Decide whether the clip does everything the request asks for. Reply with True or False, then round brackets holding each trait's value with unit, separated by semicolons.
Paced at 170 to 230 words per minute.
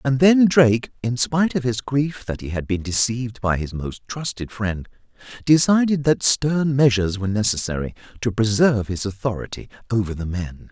True (175 wpm)